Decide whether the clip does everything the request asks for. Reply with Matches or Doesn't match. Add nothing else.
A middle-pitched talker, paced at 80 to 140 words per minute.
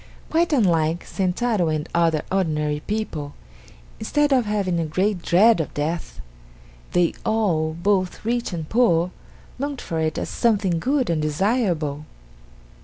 Matches